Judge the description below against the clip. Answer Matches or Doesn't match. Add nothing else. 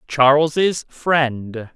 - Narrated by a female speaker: Doesn't match